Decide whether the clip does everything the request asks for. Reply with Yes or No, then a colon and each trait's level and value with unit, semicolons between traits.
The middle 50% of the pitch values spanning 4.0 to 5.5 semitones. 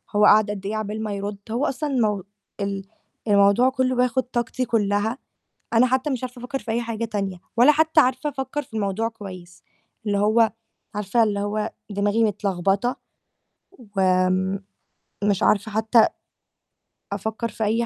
No: average, 3.3 semitones